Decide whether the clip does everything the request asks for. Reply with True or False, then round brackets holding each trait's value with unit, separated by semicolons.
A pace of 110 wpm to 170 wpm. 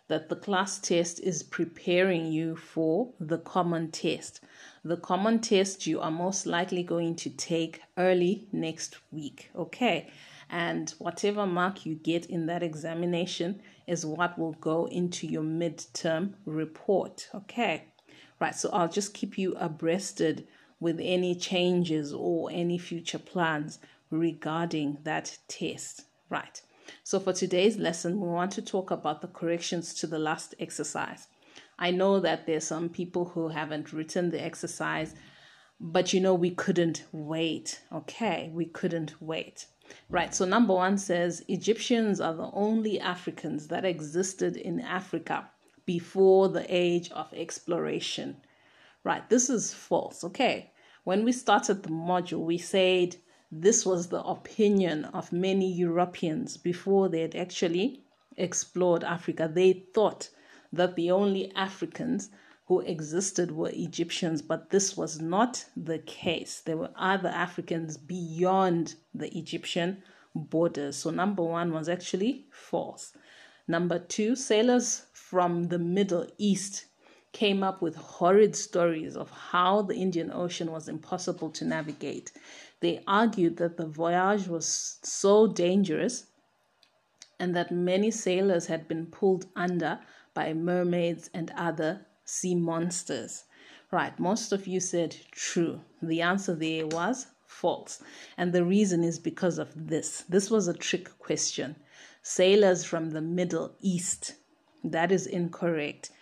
True (140 wpm)